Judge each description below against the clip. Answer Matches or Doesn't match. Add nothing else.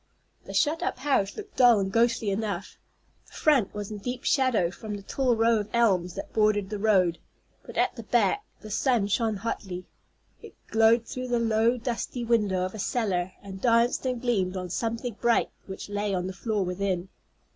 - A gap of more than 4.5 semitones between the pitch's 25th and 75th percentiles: Doesn't match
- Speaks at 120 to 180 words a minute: Doesn't match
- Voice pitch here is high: Matches